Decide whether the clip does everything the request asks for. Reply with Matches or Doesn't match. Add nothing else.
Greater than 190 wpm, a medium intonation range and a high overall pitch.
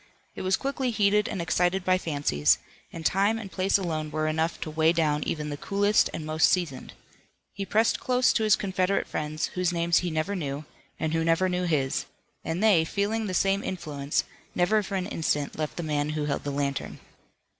Doesn't match